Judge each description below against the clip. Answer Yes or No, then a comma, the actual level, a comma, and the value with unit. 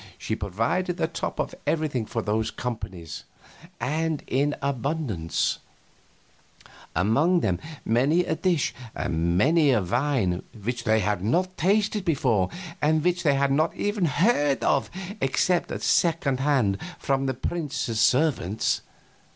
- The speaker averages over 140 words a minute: No, slow, 135 wpm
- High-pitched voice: No, low, 135 Hz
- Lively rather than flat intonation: Yes, wide, 6.6 semitones